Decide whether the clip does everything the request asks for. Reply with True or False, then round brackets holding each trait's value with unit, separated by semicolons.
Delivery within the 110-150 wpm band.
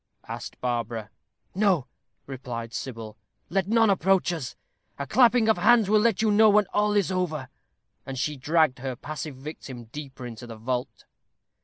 False (160 wpm)